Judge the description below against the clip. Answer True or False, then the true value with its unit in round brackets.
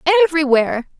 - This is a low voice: False (290 Hz)